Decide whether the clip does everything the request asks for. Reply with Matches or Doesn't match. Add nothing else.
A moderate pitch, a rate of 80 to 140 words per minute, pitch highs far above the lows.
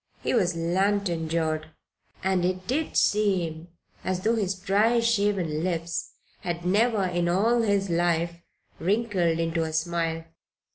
Doesn't match